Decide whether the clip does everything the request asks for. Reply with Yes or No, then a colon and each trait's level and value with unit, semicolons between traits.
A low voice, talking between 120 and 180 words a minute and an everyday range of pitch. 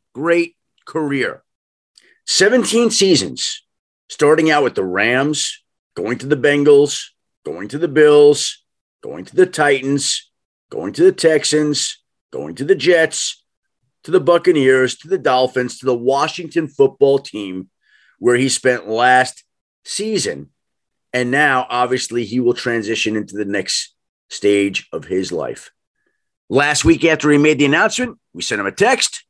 No: medium, 145 Hz; average, 145 wpm; average, 4.5 semitones